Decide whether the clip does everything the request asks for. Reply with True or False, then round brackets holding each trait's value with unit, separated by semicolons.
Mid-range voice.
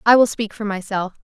False (210 Hz)